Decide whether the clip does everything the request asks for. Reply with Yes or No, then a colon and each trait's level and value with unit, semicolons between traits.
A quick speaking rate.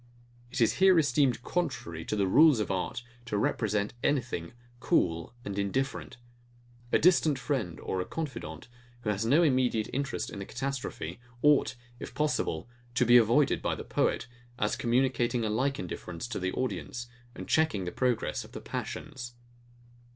No: average, 160 wpm